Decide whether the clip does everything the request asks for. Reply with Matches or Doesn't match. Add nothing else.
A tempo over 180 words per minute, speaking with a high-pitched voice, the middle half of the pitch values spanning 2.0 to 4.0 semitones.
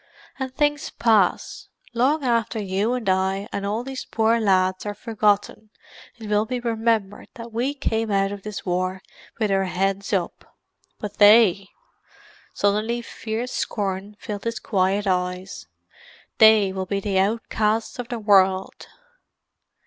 Doesn't match